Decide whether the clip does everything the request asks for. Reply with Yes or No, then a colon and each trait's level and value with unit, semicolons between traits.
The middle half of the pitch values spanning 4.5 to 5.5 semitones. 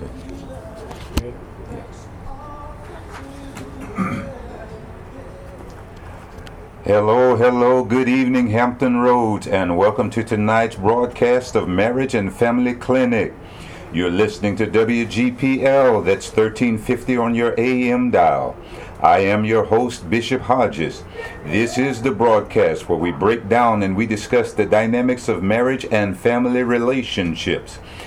No: average, 3.3 semitones